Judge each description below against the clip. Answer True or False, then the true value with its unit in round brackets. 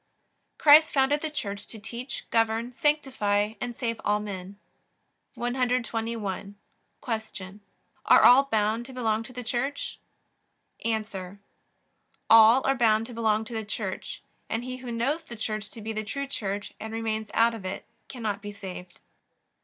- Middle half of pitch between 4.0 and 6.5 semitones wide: False (2.9 semitones)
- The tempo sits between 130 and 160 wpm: True (155 wpm)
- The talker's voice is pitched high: True (225 Hz)